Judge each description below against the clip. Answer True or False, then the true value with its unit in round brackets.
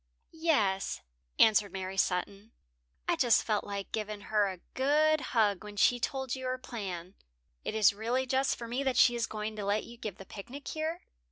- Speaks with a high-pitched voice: True (220 Hz)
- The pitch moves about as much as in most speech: True (4.4 semitones)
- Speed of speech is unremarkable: True (190 wpm)